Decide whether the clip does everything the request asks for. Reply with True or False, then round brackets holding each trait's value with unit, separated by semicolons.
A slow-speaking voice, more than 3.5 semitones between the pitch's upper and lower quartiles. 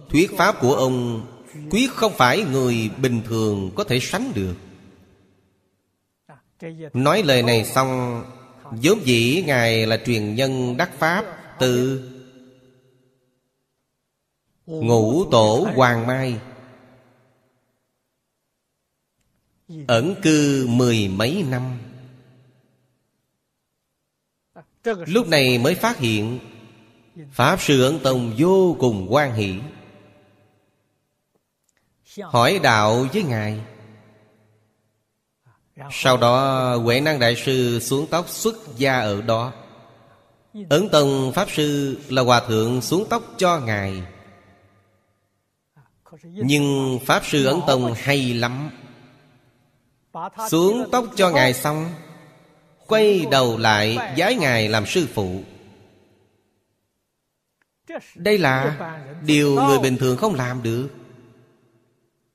True (100 wpm; 4.3 semitones)